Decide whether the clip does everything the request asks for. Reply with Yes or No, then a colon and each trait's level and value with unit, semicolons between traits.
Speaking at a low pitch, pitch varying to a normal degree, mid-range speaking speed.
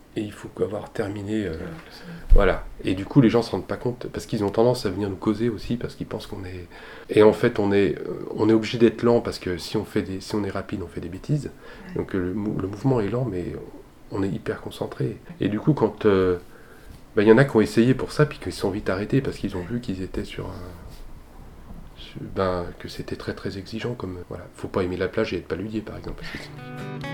No: low, 105 Hz; average, 3.7 semitones; fast, 250 wpm